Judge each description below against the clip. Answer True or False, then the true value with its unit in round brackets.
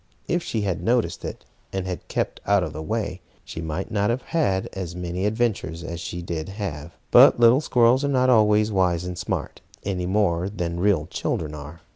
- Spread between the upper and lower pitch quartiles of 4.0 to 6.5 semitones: True (4.4 semitones)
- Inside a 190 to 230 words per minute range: True (195 wpm)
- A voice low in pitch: True (95 Hz)